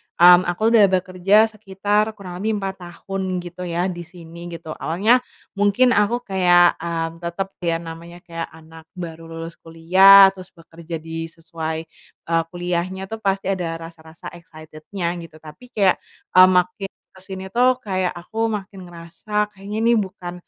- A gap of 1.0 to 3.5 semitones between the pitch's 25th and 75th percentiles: Yes, average, 2.8 semitones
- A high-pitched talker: No, medium, 180 Hz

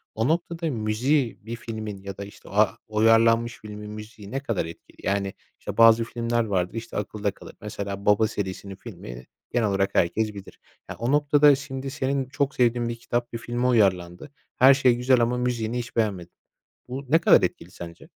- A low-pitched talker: Yes, low, 115 Hz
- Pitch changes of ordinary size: Yes, average, 3.4 semitones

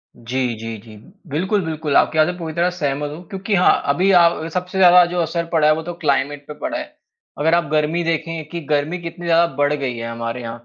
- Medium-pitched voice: Yes, medium, 160 Hz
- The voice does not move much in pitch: No, average, 3.4 semitones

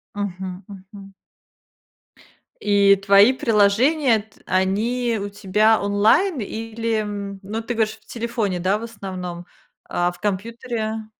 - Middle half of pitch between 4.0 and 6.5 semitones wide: No, narrow, 2.4 semitones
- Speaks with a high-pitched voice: Yes, high, 210 Hz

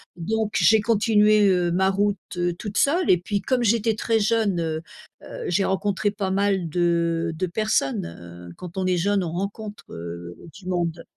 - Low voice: No, high, 190 Hz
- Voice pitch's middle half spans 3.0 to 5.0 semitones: Yes, average, 3.6 semitones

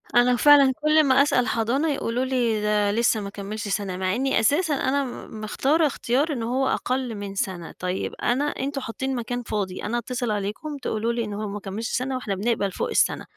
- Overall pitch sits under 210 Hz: No, high, 235 Hz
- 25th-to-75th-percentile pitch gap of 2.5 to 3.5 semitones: No, average, 4.2 semitones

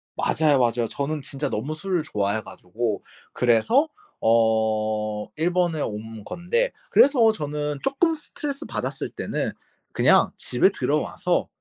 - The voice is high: No, medium, 140 Hz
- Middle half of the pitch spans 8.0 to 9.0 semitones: Yes, wide, 8.3 semitones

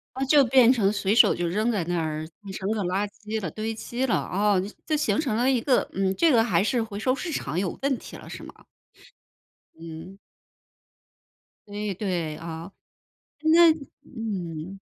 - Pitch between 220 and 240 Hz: No, high, 210 Hz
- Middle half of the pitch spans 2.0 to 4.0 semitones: No, average, 5.2 semitones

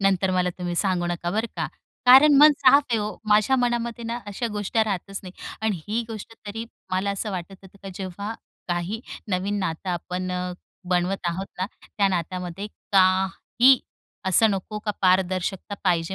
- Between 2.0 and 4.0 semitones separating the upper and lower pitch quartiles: Yes, average, 3.0 semitones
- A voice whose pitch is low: No, high, 195 Hz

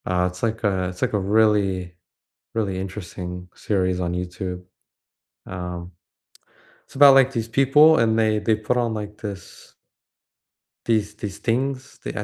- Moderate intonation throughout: Yes, average, 3.8 semitones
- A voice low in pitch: Yes, low, 105 Hz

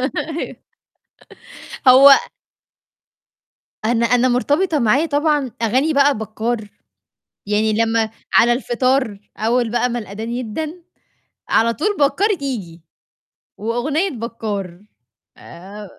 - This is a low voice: No, high, 240 Hz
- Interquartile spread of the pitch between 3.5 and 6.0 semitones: Yes, average, 4.5 semitones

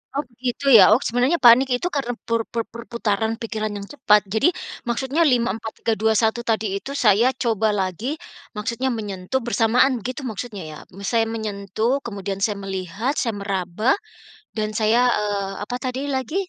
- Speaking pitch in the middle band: No, high, 225 Hz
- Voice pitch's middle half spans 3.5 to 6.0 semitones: No, average, 2.8 semitones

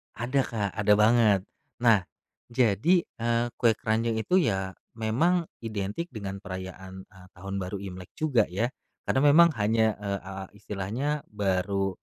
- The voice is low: Yes, low, 110 Hz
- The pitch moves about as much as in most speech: Yes, average, 3.5 semitones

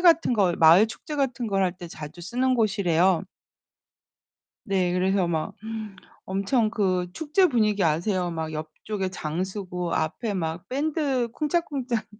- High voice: Yes, high, 195 Hz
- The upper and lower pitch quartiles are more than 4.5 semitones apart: Yes, wide, 5.6 semitones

